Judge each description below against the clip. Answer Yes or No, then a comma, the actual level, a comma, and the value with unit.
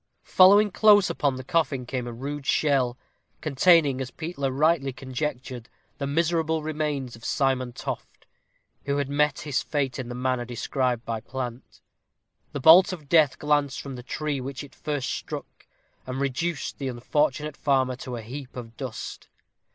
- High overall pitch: No, medium, 140 Hz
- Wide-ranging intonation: No, average, 2.9 semitones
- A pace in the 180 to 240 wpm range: No, average, 160 wpm